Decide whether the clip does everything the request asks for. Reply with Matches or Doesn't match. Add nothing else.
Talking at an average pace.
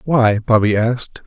Matches